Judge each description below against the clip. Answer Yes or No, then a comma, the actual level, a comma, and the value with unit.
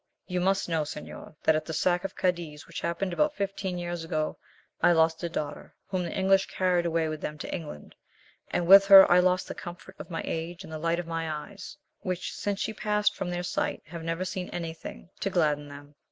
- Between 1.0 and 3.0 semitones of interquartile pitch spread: Yes, narrow, 2.5 semitones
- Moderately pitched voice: Yes, medium, 175 Hz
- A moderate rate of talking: No, fast, 220 wpm